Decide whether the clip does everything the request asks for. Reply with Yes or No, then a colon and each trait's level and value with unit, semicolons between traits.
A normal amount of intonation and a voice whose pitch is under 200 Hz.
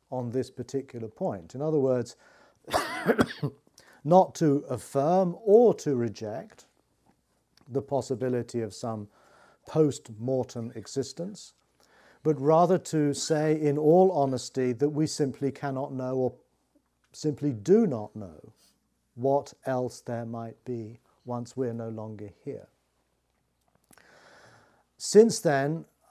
Yes: average, 4.2 semitones; low, 135 Hz